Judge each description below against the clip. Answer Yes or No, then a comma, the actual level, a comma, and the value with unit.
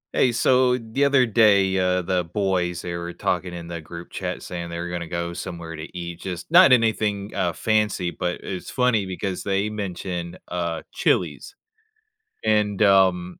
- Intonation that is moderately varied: Yes, average, 3.6 semitones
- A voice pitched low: Yes, very low, 95 Hz